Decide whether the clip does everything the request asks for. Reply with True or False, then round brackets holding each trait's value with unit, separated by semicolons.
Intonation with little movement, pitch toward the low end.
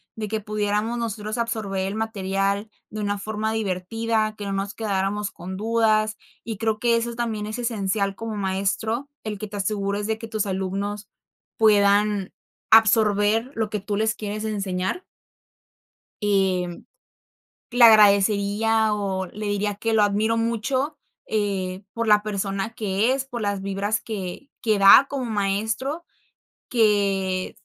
False (2.0 semitones; 210 Hz)